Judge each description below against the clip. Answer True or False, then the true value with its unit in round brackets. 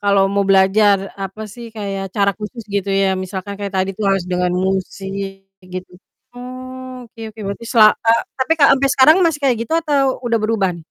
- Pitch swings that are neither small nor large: True (4.1 semitones)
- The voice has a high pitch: True (200 Hz)